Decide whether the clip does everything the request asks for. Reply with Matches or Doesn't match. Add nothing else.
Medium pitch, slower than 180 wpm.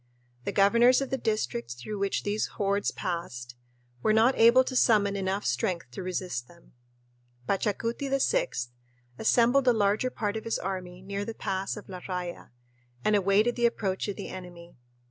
Doesn't match